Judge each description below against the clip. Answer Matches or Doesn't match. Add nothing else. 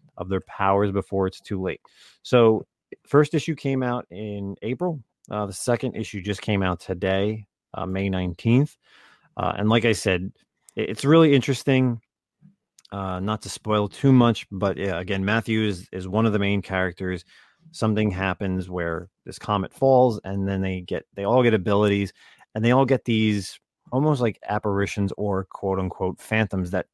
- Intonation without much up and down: Doesn't match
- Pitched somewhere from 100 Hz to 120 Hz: Matches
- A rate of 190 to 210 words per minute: Doesn't match